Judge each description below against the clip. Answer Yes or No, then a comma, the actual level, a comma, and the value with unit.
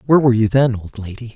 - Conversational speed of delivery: No, fast, 265 wpm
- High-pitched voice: No, low, 120 Hz